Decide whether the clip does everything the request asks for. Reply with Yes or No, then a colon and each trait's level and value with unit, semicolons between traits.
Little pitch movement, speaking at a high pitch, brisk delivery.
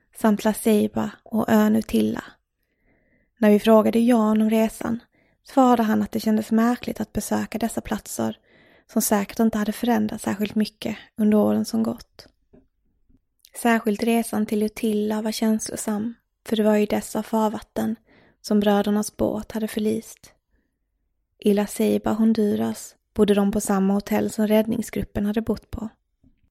No: narrow, 1.1 semitones; high, 215 Hz; average, 145 wpm